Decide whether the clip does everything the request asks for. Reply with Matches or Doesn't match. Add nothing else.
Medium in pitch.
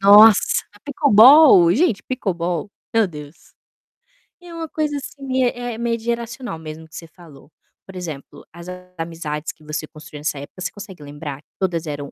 Matches